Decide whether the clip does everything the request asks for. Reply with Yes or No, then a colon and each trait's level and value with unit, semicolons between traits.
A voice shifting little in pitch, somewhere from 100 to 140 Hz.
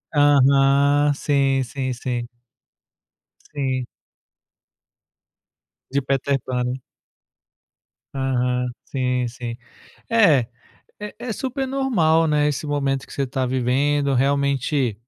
Yes: narrow, 2.3 semitones; low, 135 Hz